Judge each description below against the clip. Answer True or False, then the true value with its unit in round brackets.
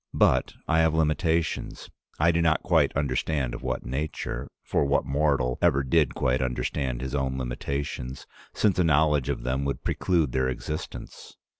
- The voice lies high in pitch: False (70 Hz)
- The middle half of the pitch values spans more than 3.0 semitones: True (3.6 semitones)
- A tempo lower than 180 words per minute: True (165 wpm)